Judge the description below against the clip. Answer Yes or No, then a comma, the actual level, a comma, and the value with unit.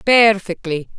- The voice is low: No, high, 200 Hz